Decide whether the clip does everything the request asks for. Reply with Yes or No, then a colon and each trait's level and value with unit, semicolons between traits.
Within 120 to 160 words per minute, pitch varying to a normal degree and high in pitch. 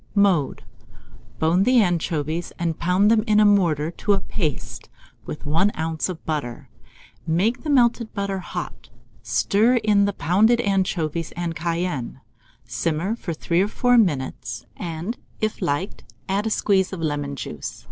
No: average, 150 wpm; average, 4.5 semitones; medium, 180 Hz